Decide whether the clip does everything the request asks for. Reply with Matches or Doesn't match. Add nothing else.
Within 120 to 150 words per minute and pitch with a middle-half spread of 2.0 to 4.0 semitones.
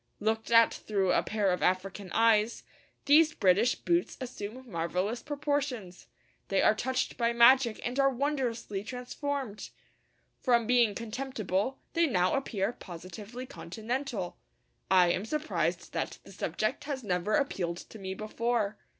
Doesn't match